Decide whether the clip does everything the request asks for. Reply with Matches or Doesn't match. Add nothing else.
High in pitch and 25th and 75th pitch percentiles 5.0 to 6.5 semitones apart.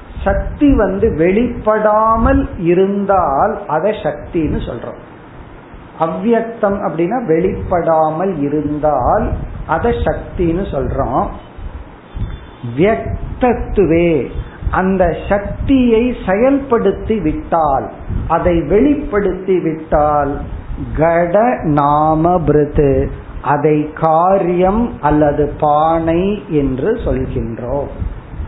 Doesn't match